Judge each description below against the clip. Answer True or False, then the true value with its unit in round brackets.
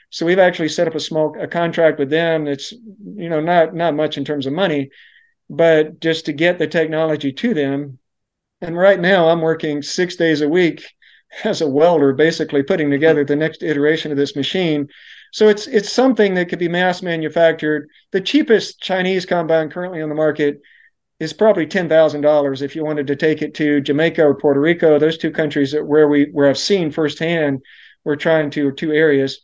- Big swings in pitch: False (2.9 semitones)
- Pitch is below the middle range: False (160 Hz)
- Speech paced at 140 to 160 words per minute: False (200 wpm)